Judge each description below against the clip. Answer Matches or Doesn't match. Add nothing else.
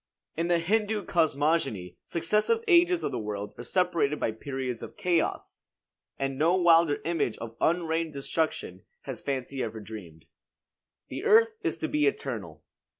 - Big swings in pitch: Matches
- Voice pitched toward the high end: Doesn't match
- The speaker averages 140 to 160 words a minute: Matches